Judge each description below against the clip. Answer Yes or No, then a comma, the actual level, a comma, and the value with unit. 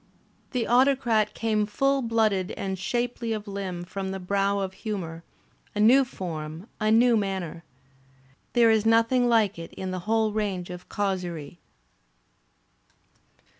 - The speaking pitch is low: No, high, 205 Hz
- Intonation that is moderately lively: Yes, average, 3.5 semitones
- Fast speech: No, slow, 135 wpm